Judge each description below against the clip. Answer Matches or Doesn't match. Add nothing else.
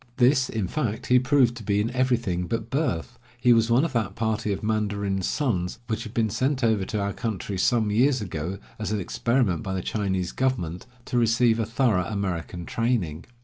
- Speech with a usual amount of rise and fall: Matches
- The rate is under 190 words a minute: Doesn't match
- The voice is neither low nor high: Doesn't match